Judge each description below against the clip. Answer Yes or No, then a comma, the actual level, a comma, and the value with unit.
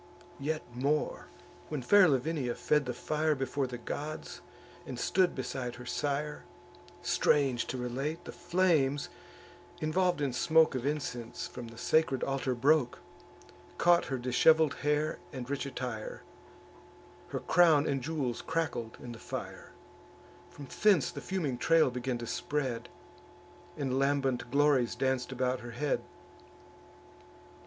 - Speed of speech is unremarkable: No, slow, 130 wpm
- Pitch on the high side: No, medium, 140 Hz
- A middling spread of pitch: Yes, average, 3.5 semitones